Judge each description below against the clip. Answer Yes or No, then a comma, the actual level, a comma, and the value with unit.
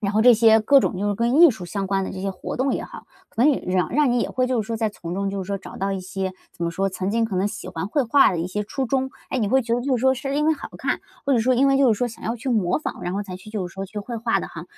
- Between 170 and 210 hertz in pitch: No, high, 220 Hz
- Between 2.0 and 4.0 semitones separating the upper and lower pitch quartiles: No, average, 4.7 semitones